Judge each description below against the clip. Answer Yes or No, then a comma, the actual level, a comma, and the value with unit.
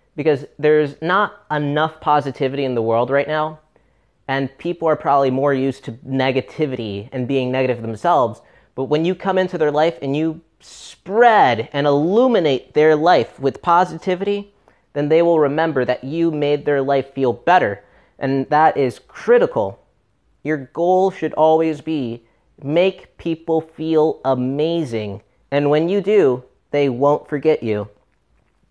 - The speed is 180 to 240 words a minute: No, average, 145 wpm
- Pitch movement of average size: Yes, average, 3.5 semitones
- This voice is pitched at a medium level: Yes, medium, 150 Hz